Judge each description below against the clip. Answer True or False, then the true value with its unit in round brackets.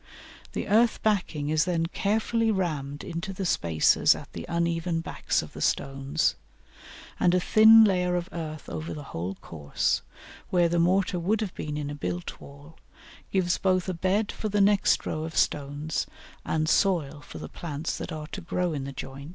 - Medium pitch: True (170 Hz)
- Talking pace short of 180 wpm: False (185 wpm)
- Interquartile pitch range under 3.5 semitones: False (4.3 semitones)